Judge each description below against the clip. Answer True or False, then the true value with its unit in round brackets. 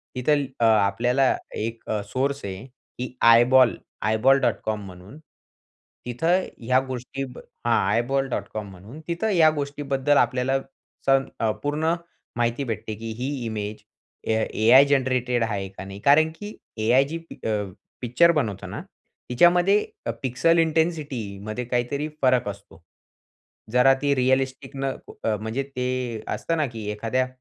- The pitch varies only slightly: False (4.1 semitones)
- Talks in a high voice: False (125 Hz)